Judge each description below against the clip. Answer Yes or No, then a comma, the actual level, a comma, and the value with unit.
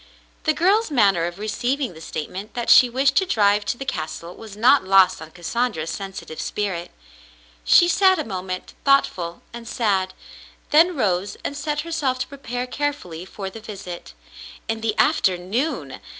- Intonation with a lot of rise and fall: Yes, wide, 6.9 semitones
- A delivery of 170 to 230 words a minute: No, average, 160 wpm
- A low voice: No, high, 215 Hz